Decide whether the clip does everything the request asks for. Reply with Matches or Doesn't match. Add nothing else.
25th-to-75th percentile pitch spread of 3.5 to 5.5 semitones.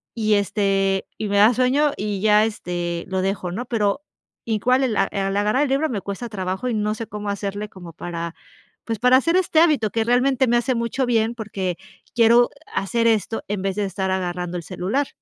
Matches